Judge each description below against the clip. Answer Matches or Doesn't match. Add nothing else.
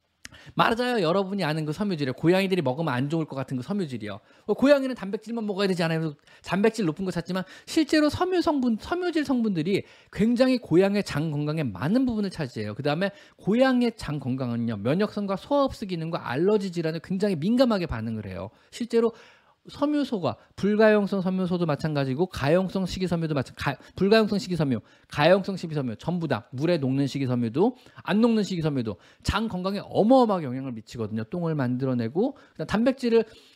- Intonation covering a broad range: Matches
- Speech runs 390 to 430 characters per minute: Matches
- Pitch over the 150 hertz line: Matches